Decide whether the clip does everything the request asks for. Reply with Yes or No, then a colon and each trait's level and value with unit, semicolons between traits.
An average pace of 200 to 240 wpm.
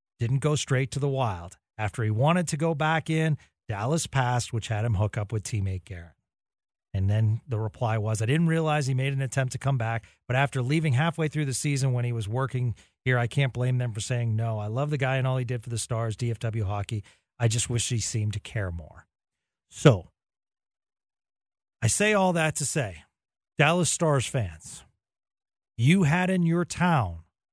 Yes: fast, 205 wpm